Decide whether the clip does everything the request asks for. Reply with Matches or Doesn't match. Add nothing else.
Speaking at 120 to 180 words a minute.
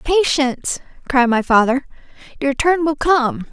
Matches